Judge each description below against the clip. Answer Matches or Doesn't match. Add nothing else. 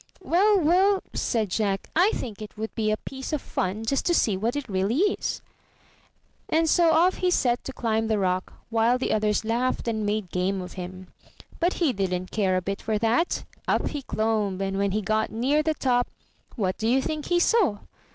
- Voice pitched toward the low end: Doesn't match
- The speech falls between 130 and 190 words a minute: Doesn't match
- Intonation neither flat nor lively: Doesn't match